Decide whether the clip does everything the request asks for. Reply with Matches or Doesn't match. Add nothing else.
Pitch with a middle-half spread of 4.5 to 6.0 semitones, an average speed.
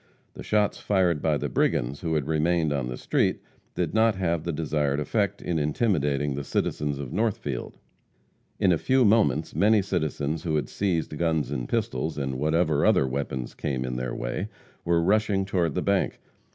Matches